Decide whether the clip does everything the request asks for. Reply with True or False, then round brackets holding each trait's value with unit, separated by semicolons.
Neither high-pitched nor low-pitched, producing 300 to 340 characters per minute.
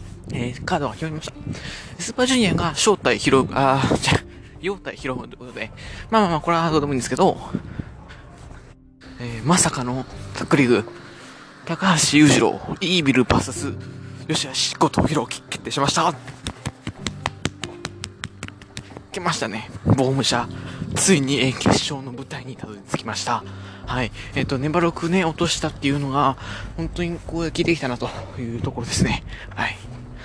False (130 Hz; 310 characters per minute)